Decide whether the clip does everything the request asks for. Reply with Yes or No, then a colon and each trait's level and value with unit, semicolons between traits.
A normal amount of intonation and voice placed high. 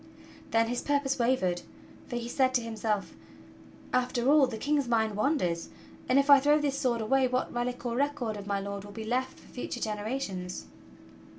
Yes: average, 3.9 semitones; high, 245 Hz